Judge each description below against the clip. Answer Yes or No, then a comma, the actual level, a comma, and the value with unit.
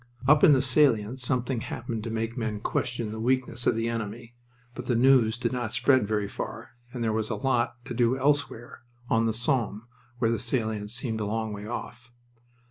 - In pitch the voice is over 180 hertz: No, low, 115 Hz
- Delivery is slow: No, average, 200 wpm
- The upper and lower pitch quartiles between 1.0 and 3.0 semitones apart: Yes, narrow, 2.4 semitones